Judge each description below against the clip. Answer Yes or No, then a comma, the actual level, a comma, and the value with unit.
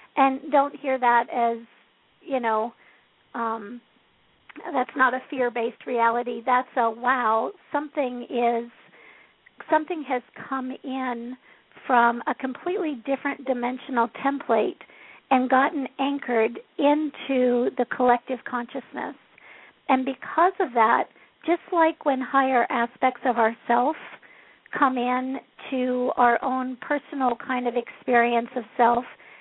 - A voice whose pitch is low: No, very high, 255 Hz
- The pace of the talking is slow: Yes, slow, 120 wpm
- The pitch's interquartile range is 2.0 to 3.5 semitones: Yes, narrow, 2.5 semitones